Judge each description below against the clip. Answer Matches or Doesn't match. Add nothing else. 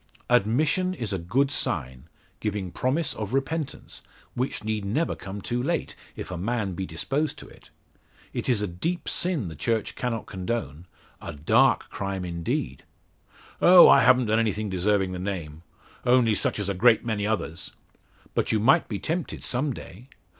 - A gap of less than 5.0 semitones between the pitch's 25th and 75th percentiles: Doesn't match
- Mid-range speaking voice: Doesn't match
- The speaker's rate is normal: Matches